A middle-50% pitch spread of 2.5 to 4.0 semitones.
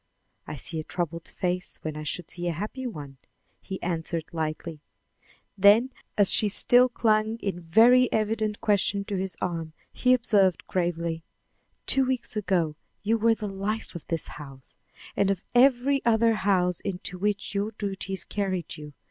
No: average, 4.5 semitones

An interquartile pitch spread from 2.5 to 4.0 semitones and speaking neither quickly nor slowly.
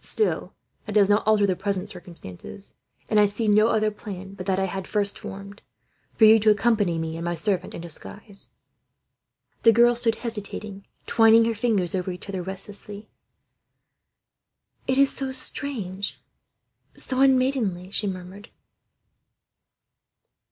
Yes: average, 2.9 semitones; average, 145 wpm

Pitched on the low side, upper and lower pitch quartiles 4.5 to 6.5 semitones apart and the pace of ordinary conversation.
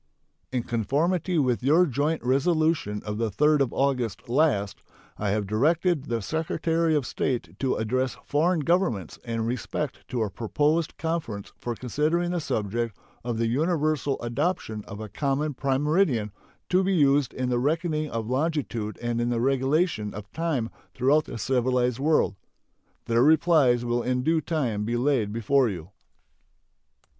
Yes: low, 130 Hz; average, 5.1 semitones; average, 155 wpm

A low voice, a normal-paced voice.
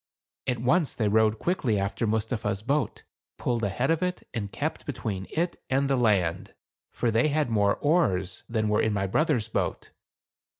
Yes: low, 115 Hz; average, 170 wpm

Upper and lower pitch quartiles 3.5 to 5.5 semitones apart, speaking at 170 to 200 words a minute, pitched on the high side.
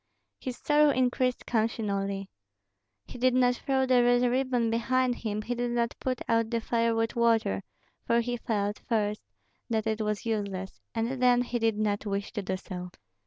No: average, 2.7 semitones; average, 175 wpm; high, 230 Hz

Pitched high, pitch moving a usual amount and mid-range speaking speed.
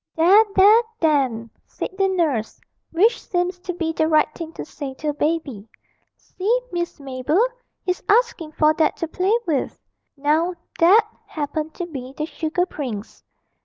Yes: very high, 320 Hz; average, 3.7 semitones; average, 160 wpm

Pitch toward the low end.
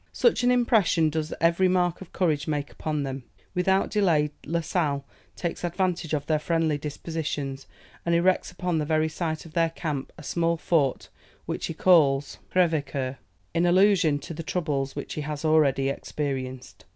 No: medium, 160 Hz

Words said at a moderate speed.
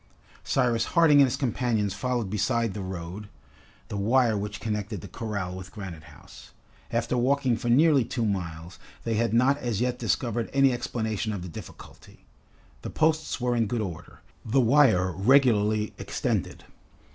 Yes: average, 155 wpm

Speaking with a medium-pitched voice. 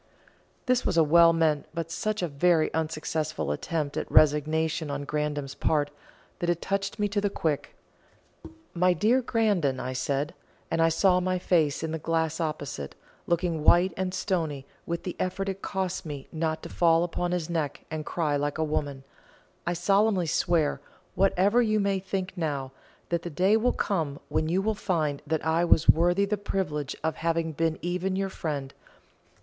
Yes: medium, 165 Hz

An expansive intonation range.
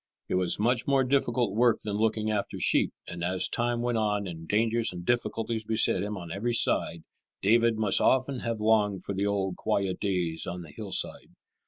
No: average, 3.6 semitones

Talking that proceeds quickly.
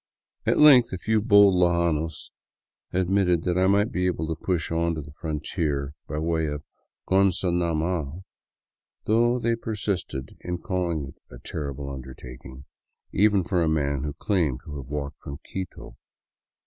No: average, 160 wpm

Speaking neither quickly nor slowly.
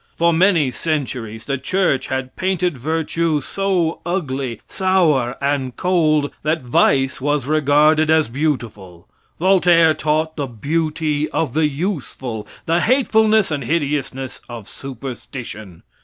No: slow, 120 wpm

